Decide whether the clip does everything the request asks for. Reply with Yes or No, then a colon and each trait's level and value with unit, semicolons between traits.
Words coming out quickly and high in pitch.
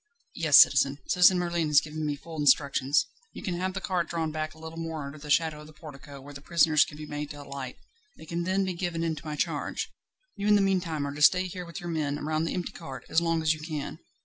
No: fast, 255 wpm; medium, 160 Hz